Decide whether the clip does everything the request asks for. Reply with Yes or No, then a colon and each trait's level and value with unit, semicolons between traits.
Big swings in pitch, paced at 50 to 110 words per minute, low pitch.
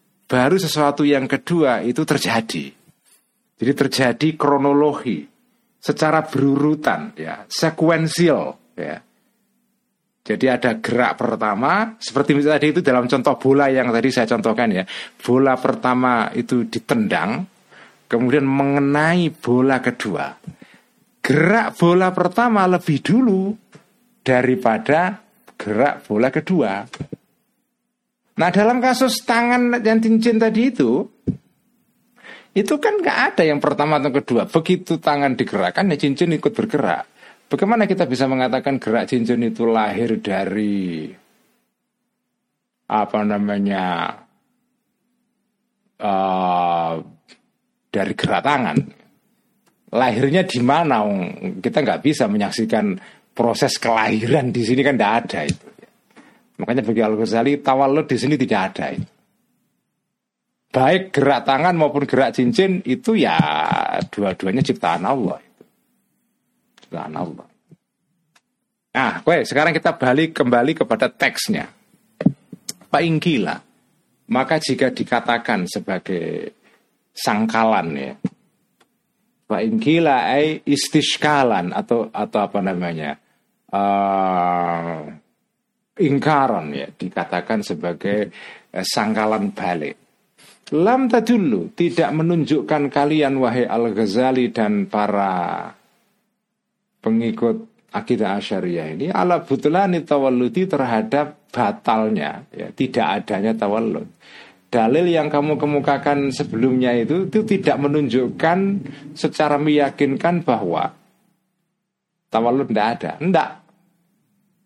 No: wide, 7.5 semitones; average, 100 wpm; medium, 145 Hz